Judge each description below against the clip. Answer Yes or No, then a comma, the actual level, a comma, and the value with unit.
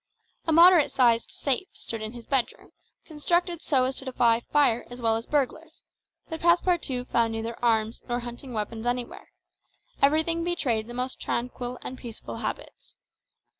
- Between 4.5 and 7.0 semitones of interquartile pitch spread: Yes, average, 4.9 semitones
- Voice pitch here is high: Yes, very high, 250 Hz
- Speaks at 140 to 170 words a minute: Yes, average, 155 wpm